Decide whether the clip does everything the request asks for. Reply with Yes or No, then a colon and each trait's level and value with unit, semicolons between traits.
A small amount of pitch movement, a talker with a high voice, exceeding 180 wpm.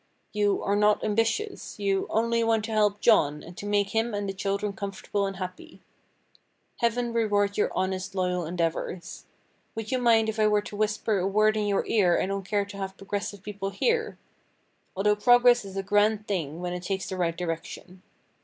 Yes: narrow, 2.2 semitones; high, 205 Hz; average, 190 wpm